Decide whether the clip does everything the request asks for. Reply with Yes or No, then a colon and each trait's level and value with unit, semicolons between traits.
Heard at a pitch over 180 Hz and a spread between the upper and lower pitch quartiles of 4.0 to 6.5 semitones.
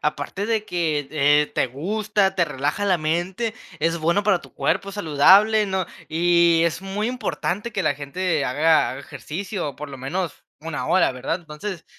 No: medium, 170 Hz; average, 4.6 semitones